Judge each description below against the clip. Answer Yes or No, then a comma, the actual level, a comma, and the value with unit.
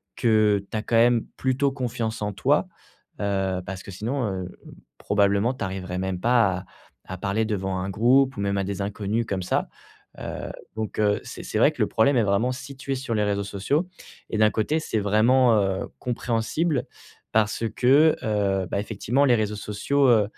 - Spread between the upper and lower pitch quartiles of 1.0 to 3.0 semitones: No, average, 3.8 semitones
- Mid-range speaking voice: No, low, 110 Hz